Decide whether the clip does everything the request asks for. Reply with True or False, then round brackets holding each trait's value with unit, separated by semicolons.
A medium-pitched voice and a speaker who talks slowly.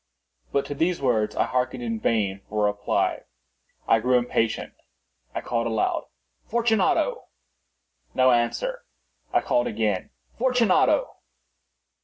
False (125 Hz; 120 wpm)